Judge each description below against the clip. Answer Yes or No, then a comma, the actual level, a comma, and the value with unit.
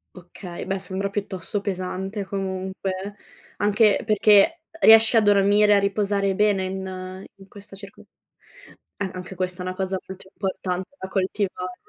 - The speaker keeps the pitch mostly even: Yes, narrow, 1.5 semitones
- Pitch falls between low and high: No, high, 195 Hz